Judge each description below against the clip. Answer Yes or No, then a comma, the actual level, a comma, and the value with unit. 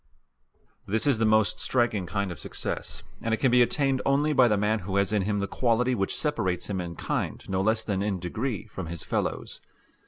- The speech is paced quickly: Yes, fast, 215 wpm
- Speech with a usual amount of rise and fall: Yes, average, 4.0 semitones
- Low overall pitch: Yes, low, 105 Hz